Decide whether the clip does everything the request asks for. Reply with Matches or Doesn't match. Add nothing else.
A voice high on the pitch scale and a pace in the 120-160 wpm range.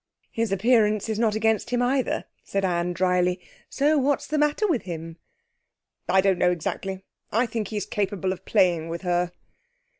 Doesn't match